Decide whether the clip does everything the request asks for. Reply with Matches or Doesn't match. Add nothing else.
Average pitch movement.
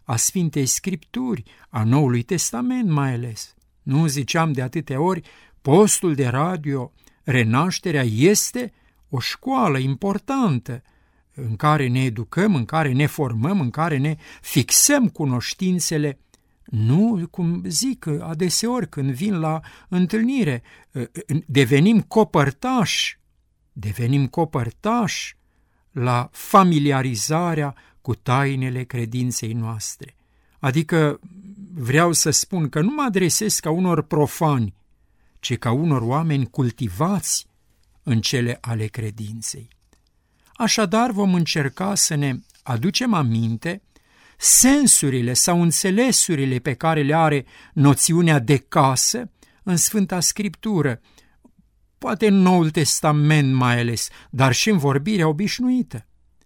Doesn't match